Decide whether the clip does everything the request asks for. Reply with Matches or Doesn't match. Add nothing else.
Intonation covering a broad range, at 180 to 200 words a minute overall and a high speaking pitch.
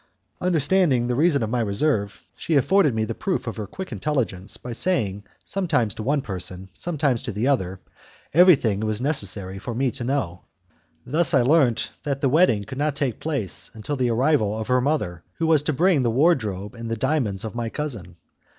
Doesn't match